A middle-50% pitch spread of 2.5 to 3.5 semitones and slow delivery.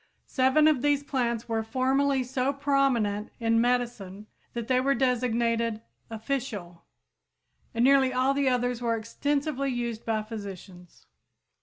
Yes: average, 3.1 semitones; slow, 130 wpm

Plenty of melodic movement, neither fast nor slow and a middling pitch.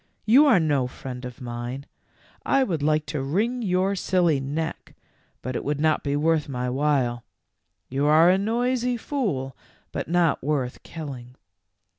Yes: wide, 5.7 semitones; average, 155 wpm; medium, 150 Hz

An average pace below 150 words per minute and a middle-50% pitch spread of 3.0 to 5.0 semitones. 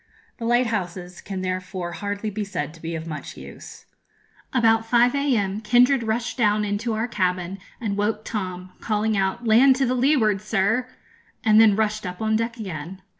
No: average, 170 wpm; average, 3.5 semitones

